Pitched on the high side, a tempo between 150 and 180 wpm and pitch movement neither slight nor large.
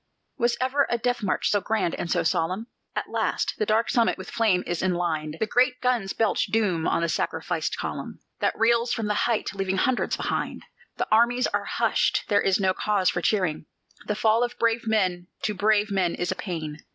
No: high, 210 Hz; average, 200 wpm; average, 4.2 semitones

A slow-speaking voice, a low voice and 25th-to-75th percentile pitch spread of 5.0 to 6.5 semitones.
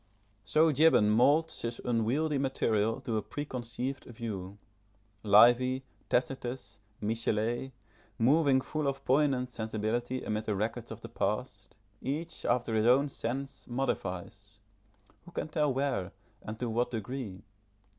No: slow, 125 wpm; low, 120 Hz; average, 3.8 semitones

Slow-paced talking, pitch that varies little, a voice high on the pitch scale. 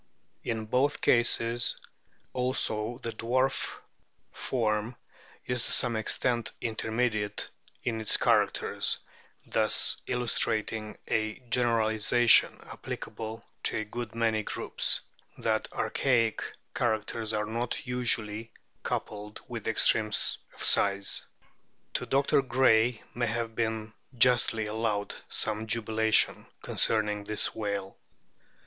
No: slow, 105 wpm; narrow, 1.9 semitones; low, 110 Hz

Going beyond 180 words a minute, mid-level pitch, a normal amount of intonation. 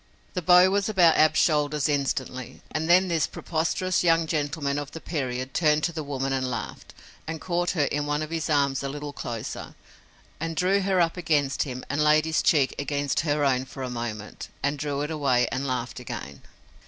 Yes: average, 200 wpm; medium, 150 Hz; average, 3.2 semitones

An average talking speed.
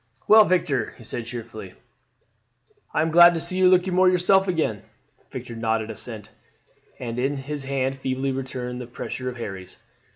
Yes: average, 160 wpm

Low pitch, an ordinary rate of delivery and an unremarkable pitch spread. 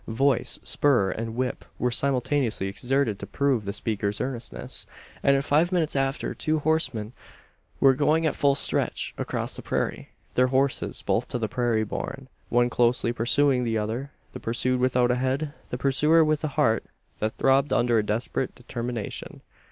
Yes: low, 125 Hz; average, 165 wpm; average, 3.3 semitones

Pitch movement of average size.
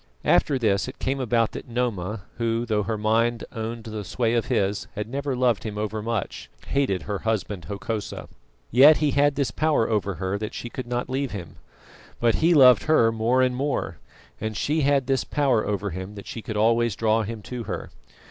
Yes: average, 3.4 semitones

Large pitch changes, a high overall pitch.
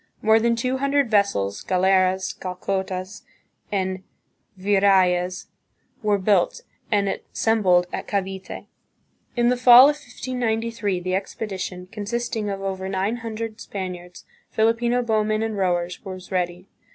No: average, 3.3 semitones; high, 200 Hz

